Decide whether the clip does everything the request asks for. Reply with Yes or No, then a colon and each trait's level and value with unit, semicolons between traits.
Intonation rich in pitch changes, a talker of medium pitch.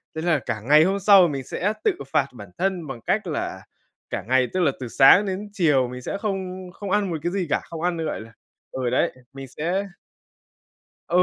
Yes: wide, 6.2 semitones; medium, 165 Hz